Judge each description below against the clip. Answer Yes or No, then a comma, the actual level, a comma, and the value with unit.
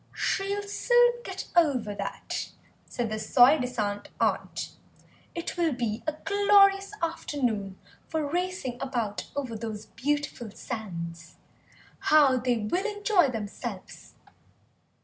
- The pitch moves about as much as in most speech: No, wide, 8.6 semitones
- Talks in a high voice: Yes, very high, 265 Hz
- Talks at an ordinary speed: No, slow, 110 wpm